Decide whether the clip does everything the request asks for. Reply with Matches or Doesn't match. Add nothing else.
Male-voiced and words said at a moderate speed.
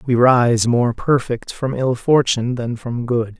Matches